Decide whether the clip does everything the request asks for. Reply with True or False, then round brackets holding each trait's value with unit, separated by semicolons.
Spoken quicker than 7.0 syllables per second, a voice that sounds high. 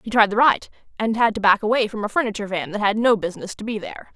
True (7.3 syllables/s; 215 Hz)